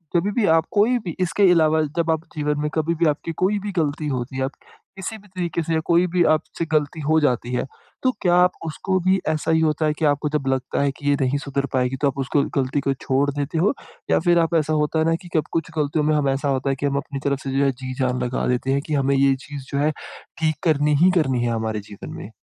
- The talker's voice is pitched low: No, medium, 150 Hz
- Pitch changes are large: No, average, 3.3 semitones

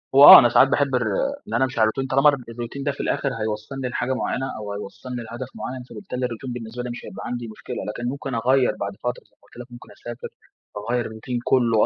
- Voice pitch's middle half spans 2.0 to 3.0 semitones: Yes, narrow, 2.5 semitones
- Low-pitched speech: Yes, low, 120 Hz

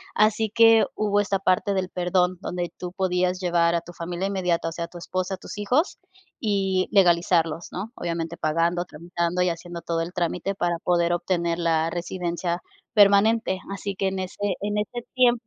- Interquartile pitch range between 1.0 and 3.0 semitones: Yes, narrow, 2.5 semitones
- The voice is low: No, medium, 180 Hz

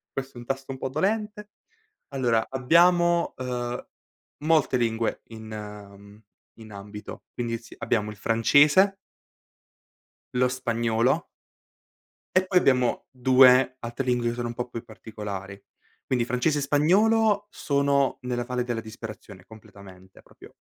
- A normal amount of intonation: Yes, average, 3.8 semitones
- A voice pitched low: Yes, low, 125 Hz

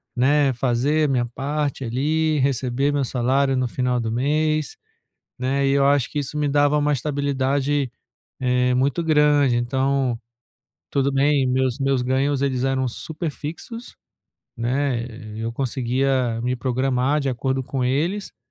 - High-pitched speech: No, low, 135 Hz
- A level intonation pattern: Yes, narrow, 2.3 semitones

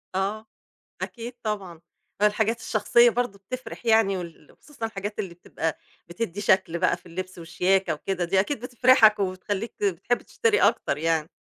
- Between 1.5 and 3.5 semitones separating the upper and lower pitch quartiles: No, average, 4.0 semitones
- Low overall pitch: No, high, 200 Hz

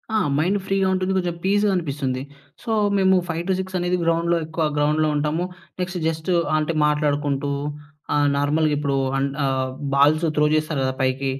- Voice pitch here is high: No, medium, 155 Hz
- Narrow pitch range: No, average, 3.7 semitones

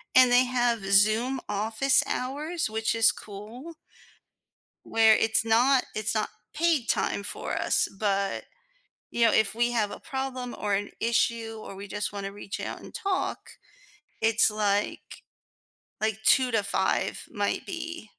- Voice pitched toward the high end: Yes, high, 225 Hz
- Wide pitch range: No, average, 3.6 semitones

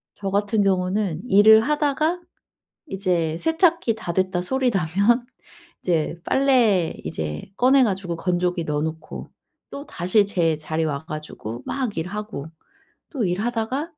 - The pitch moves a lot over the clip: Yes, wide, 6.2 semitones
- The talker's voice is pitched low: No, high, 195 Hz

